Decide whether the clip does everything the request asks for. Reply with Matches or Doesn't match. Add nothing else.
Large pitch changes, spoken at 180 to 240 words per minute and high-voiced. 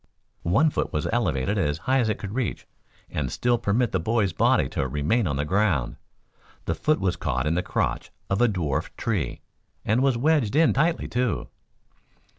Doesn't match